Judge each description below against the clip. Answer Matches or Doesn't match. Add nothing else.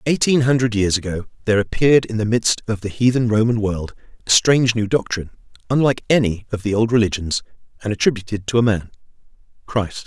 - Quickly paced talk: Doesn't match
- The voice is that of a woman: Doesn't match